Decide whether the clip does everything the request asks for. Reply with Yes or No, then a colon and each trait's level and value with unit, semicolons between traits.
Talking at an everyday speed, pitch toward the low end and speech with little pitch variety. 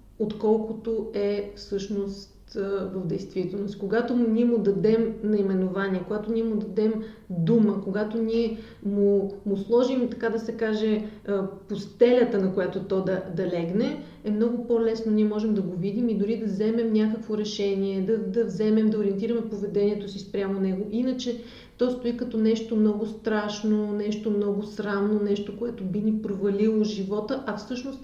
No: average, 155 wpm; high, 215 Hz; narrow, 1.9 semitones